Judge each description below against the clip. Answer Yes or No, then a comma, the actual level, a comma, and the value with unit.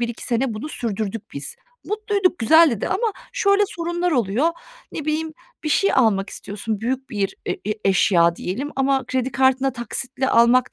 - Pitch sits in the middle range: No, very high, 260 Hz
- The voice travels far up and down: Yes, wide, 6.1 semitones